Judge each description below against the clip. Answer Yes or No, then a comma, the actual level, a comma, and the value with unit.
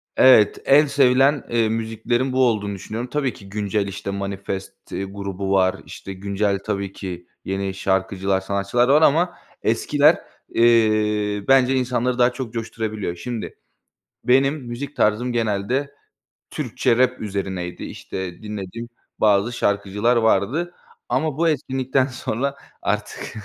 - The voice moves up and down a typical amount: Yes, average, 4.5 semitones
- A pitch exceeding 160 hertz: No, low, 110 Hz